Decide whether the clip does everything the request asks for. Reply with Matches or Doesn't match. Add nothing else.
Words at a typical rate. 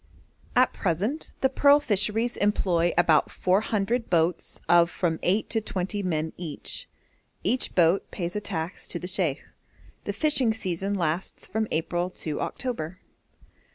Matches